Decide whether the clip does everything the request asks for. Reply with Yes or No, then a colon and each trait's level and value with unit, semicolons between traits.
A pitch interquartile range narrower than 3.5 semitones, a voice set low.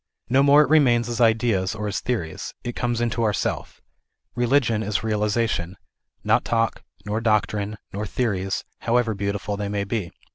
Yes: average, 2.7 semitones; low, 110 Hz